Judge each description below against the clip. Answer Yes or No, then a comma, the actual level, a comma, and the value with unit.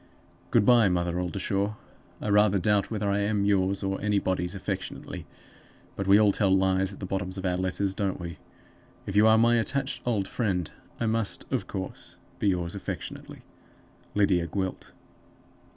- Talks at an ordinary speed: Yes, average, 165 wpm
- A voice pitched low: Yes, low, 100 Hz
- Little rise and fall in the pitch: Yes, narrow, 1.8 semitones